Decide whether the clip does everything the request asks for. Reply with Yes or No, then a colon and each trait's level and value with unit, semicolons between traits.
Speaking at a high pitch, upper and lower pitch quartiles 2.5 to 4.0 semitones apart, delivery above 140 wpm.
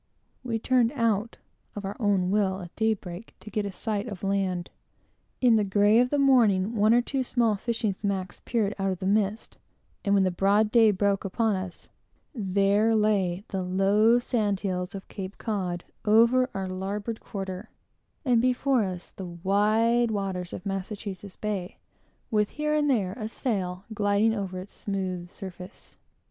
Yes: high, 205 Hz; average, 2.9 semitones; average, 165 wpm